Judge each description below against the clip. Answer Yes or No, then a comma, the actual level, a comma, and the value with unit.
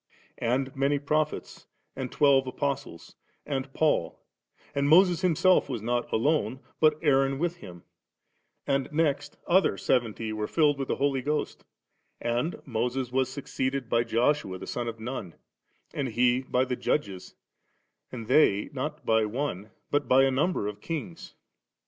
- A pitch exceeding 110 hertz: Yes, low, 135 Hz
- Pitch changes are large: No, average, 3.7 semitones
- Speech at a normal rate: Yes, average, 150 wpm